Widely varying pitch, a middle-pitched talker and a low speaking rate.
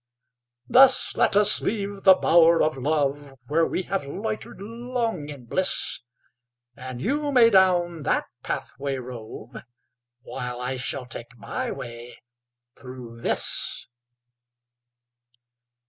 Yes: wide, 7.7 semitones; medium, 155 Hz; slow, 115 wpm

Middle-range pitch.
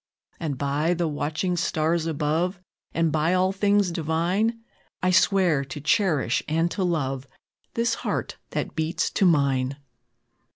Yes: medium, 165 Hz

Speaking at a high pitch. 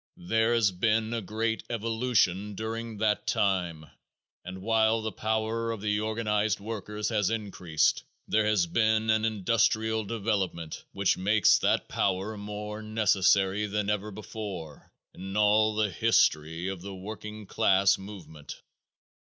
No: low, 105 Hz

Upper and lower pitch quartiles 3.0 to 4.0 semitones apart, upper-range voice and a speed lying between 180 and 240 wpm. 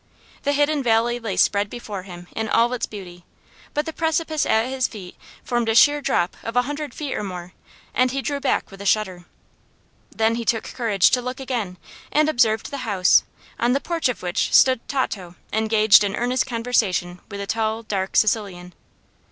No: average, 4.5 semitones; high, 225 Hz; average, 190 wpm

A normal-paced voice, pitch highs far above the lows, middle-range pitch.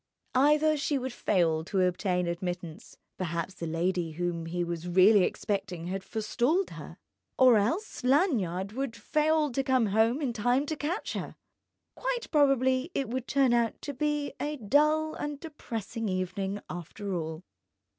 No: average, 155 wpm; wide, 7.9 semitones; high, 225 Hz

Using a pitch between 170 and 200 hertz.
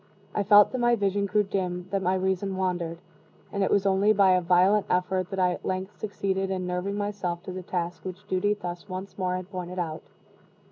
Yes: high, 190 Hz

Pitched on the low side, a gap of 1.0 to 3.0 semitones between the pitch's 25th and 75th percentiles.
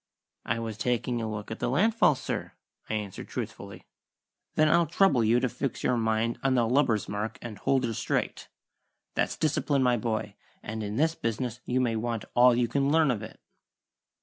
No: low, 120 Hz; average, 3.5 semitones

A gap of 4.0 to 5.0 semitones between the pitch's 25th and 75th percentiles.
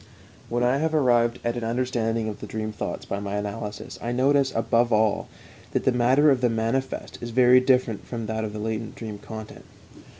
No: narrow, 2.5 semitones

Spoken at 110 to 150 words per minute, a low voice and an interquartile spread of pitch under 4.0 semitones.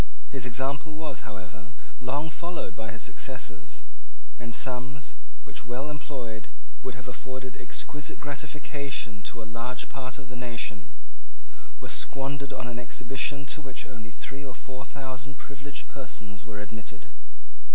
Yes: average, 140 wpm; low, 130 Hz; average, 3.4 semitones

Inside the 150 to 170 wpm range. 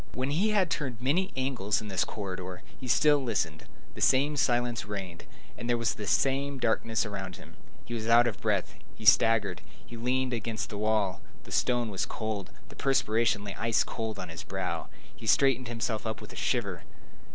No: average, 190 wpm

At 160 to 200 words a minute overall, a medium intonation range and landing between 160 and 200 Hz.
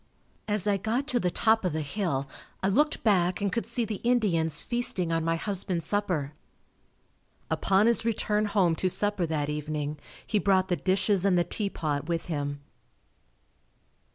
Yes: average, 165 wpm; average, 4.3 semitones; high, 190 Hz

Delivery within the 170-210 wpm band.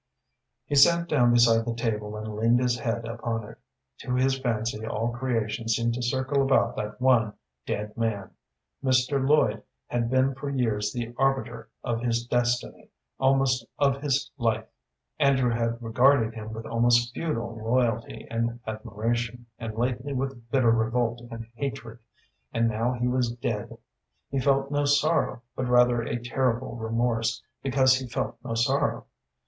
No: average, 155 wpm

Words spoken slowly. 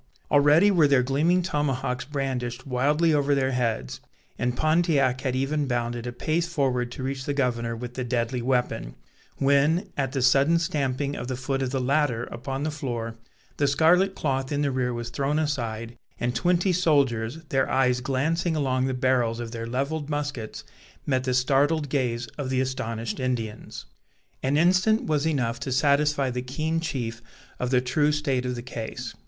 No: average, 175 wpm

